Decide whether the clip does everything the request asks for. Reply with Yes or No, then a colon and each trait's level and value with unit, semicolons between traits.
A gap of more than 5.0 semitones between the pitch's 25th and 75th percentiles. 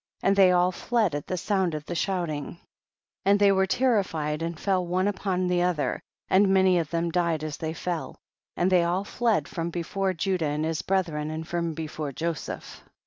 No: average, 3.0 semitones